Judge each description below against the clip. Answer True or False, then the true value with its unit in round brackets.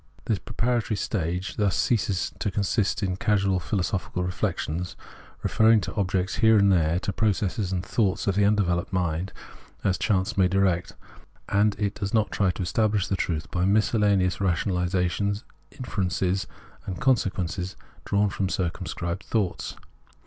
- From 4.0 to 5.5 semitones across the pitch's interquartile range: False (2.4 semitones)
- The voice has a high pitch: False (95 Hz)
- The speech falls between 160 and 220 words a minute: False (150 wpm)